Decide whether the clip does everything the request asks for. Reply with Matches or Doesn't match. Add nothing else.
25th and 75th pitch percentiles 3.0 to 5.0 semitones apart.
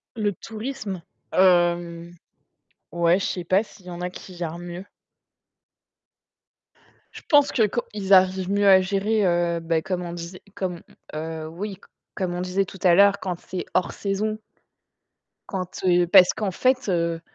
Doesn't match